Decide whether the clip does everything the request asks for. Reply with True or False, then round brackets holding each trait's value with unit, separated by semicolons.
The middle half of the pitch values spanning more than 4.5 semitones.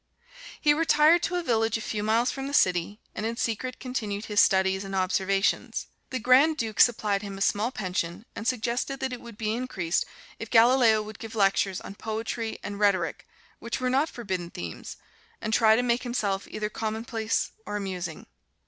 False (3.8 semitones)